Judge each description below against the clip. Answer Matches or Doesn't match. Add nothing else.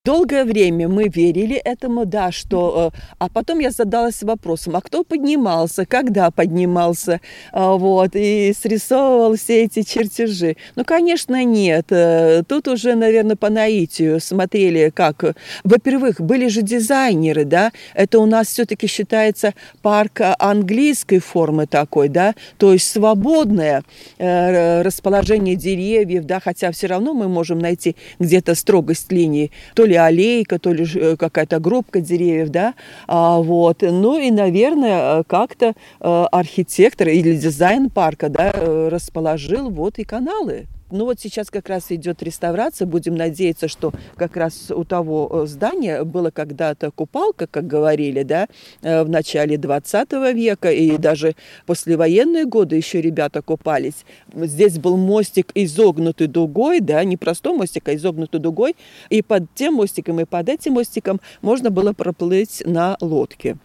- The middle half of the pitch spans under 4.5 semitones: Doesn't match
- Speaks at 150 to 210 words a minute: Doesn't match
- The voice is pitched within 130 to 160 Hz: Doesn't match